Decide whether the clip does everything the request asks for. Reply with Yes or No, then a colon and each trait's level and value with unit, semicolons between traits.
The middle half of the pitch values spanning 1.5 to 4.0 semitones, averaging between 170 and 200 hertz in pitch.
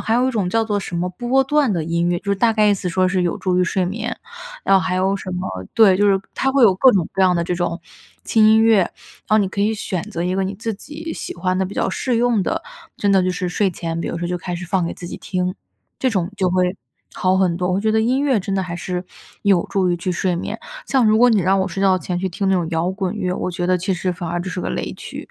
Yes: average, 3.0 semitones; high, 190 Hz